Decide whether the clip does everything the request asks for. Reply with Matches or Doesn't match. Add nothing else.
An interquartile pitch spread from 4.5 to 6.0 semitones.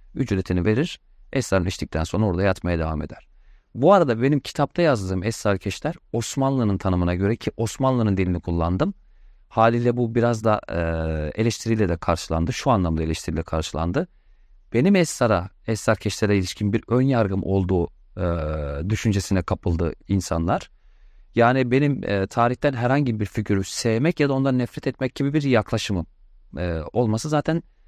Matches